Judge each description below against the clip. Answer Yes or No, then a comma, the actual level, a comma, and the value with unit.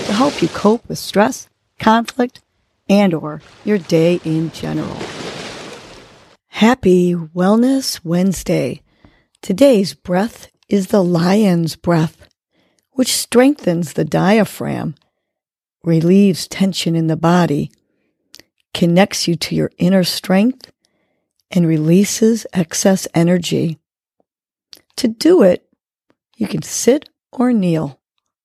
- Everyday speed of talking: No, slow, 105 wpm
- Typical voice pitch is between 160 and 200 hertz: Yes, medium, 185 Hz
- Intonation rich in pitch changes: No, average, 4.6 semitones